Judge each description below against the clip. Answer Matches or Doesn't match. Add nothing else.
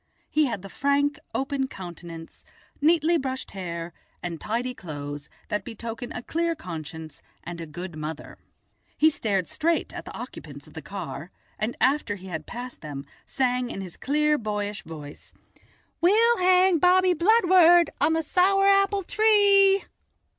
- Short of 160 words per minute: Matches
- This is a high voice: Matches